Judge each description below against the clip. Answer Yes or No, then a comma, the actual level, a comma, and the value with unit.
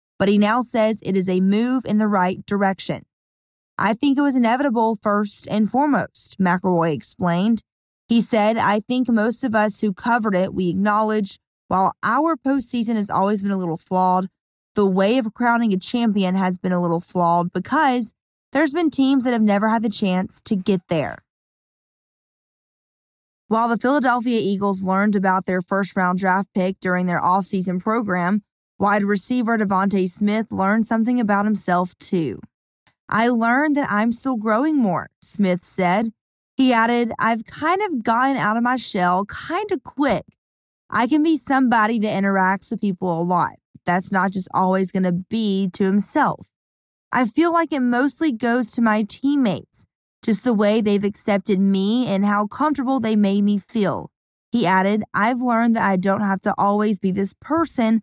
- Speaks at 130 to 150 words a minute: No, average, 175 wpm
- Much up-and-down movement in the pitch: No, average, 3.8 semitones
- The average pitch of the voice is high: Yes, high, 210 Hz